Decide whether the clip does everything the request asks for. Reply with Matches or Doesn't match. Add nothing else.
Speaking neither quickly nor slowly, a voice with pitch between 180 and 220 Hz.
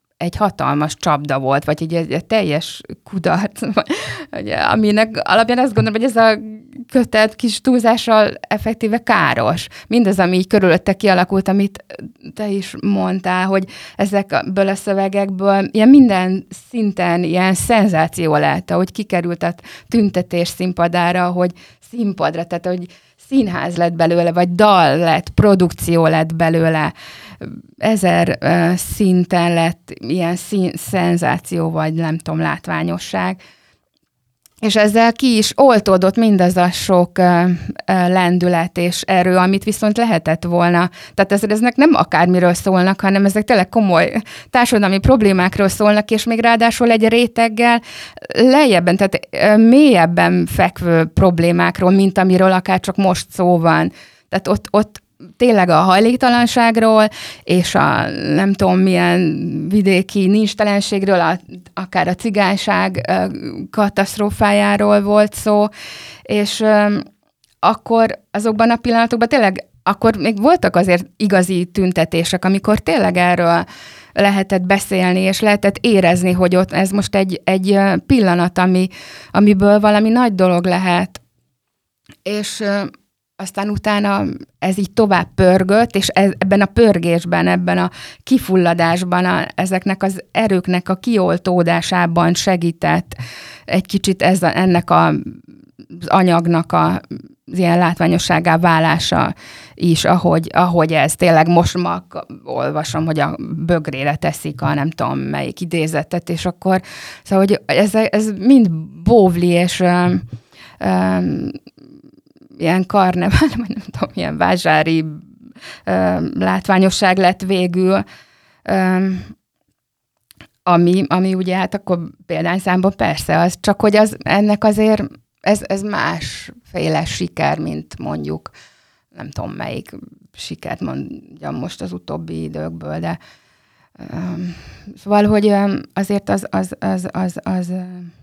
Matches